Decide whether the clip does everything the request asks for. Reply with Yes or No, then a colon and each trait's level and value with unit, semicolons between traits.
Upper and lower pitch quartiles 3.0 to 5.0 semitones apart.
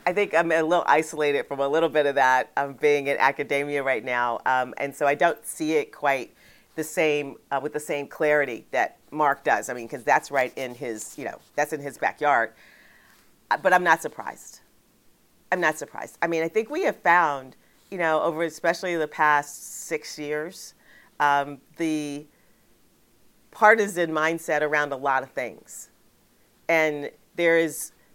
No: narrow, 2.6 semitones